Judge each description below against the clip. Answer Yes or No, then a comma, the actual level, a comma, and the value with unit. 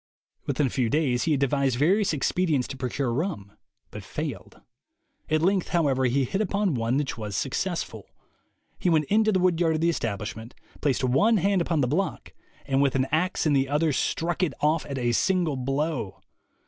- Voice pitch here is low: No, medium, 150 Hz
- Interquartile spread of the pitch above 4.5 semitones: Yes, average, 5.0 semitones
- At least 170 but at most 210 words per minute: Yes, average, 190 wpm